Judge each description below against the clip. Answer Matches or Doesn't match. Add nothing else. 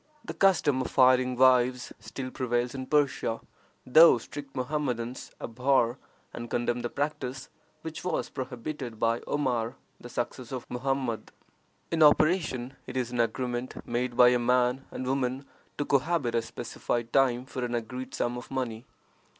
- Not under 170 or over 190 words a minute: Doesn't match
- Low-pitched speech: Matches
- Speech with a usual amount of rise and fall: Doesn't match